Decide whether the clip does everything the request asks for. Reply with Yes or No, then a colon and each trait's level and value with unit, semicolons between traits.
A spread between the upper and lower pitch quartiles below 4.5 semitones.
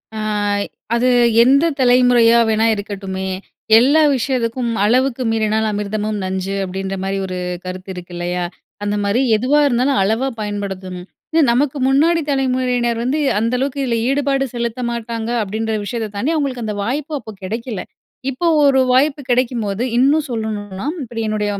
Yes: average, 4.1 semitones